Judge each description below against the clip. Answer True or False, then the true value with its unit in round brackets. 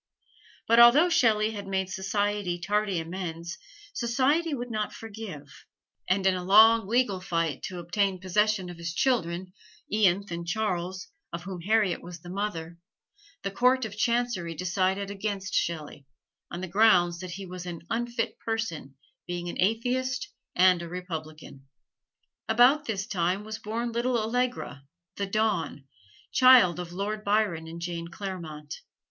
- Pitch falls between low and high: False (195 Hz)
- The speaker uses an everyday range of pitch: True (4.2 semitones)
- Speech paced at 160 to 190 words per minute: False (145 wpm)